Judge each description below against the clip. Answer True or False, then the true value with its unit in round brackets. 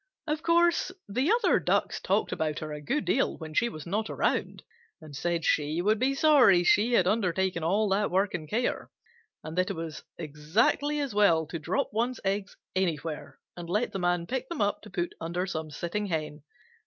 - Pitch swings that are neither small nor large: False (5.7 semitones)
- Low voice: False (185 Hz)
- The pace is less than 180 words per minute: False (195 wpm)